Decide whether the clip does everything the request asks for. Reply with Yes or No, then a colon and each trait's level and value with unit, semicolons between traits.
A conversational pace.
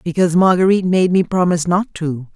Yes: average, 180 wpm